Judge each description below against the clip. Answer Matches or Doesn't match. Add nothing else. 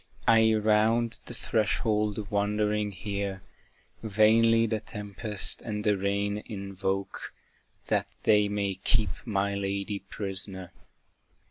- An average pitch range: Doesn't match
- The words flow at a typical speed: Doesn't match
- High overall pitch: Doesn't match